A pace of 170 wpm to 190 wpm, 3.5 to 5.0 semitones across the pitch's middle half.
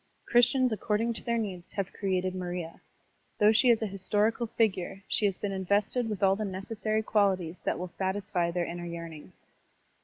No: average, 175 wpm; average, 3.1 semitones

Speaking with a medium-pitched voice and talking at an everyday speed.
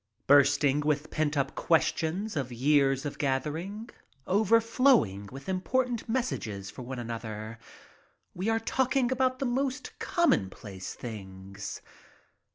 No: medium, 150 Hz; slow, 115 wpm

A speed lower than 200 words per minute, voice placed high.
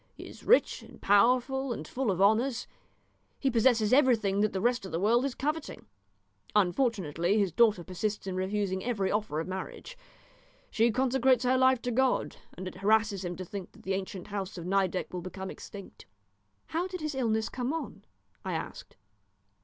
Yes: average, 180 wpm; high, 215 Hz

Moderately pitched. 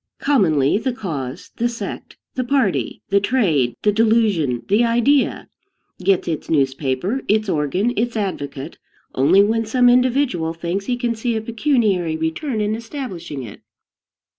No: high, 205 Hz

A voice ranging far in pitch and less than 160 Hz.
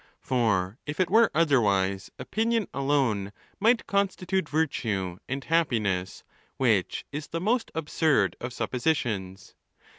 Yes: wide, 8.7 semitones; medium, 140 Hz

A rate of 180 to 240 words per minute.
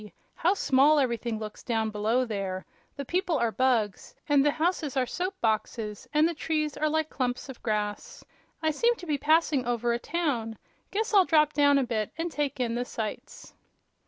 Yes: average, 190 wpm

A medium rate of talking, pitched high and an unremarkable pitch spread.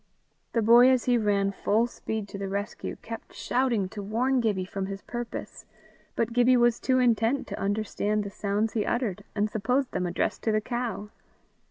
Yes: average, 185 wpm; high, 220 Hz; average, 3.1 semitones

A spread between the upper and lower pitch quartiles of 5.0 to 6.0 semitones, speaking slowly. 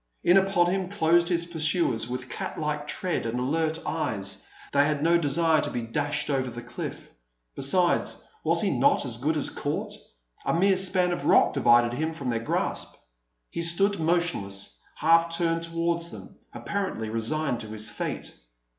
No: average, 5.3 semitones; average, 170 wpm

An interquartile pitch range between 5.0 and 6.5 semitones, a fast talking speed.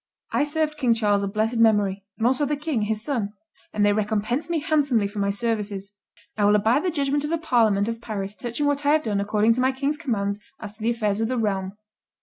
Yes: wide, 5.4 semitones; fast, 235 wpm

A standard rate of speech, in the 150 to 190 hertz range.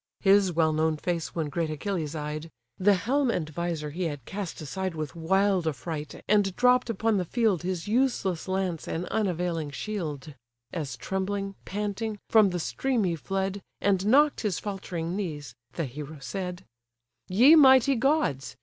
Yes: average, 160 wpm; medium, 185 Hz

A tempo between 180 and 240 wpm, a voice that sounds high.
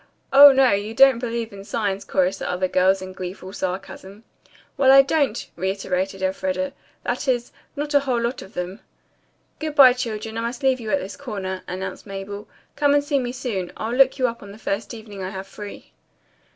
Yes: average, 190 wpm; high, 215 Hz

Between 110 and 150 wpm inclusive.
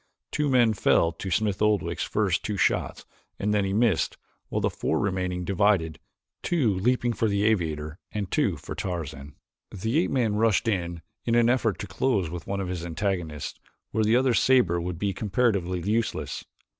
No: average, 180 wpm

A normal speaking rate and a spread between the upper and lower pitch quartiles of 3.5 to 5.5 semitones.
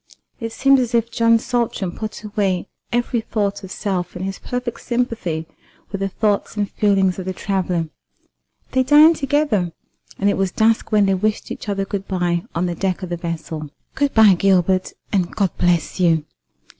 Yes: average, 180 wpm; average, 4.0 semitones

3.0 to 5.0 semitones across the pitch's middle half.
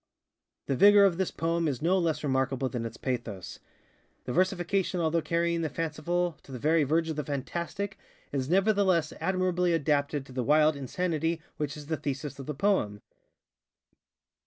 Yes: average, 4.0 semitones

